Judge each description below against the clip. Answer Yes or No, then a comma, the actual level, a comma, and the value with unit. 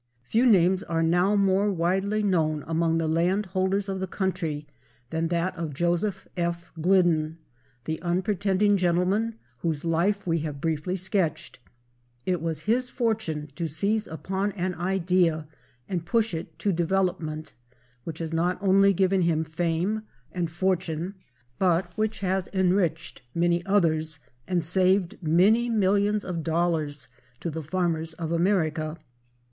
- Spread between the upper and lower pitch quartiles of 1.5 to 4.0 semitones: Yes, average, 2.9 semitones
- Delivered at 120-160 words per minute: Yes, average, 140 wpm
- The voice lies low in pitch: No, medium, 175 Hz